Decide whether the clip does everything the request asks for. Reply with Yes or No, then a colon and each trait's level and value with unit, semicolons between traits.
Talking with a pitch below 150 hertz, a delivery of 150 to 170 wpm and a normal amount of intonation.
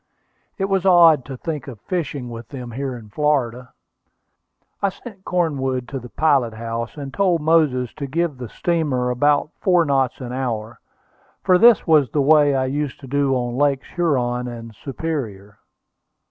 Yes: low, 135 Hz; average, 165 wpm; average, 4.3 semitones